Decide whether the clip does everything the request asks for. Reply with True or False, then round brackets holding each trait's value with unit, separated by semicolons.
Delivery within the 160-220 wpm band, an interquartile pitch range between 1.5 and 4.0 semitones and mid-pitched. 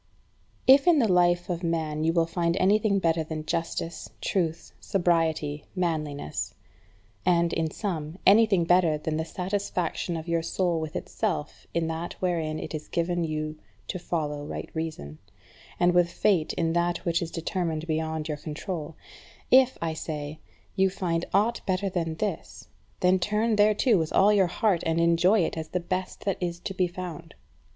True (170 wpm; 2.7 semitones; 170 Hz)